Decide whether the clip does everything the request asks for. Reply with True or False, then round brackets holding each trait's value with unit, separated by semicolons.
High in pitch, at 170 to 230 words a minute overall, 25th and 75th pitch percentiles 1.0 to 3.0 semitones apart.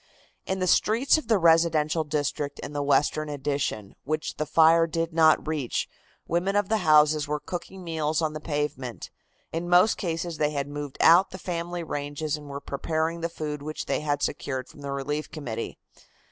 False (155 Hz; 185 wpm; 2.5 semitones)